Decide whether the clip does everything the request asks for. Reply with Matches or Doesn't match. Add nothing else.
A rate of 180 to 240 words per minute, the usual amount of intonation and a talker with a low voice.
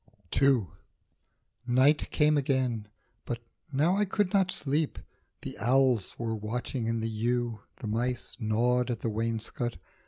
Doesn't match